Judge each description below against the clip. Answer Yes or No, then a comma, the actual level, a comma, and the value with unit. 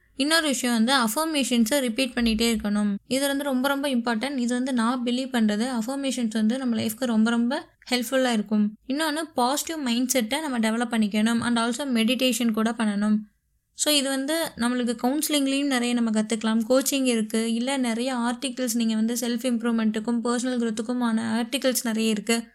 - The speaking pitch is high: Yes, high, 240 Hz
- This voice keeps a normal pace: No, fast, 155 wpm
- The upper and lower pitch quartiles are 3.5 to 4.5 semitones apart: No, narrow, 2.6 semitones